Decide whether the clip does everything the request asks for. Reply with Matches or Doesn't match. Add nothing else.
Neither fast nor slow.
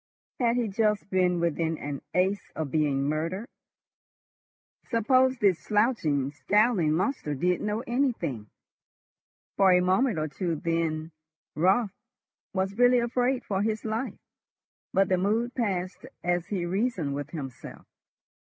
Doesn't match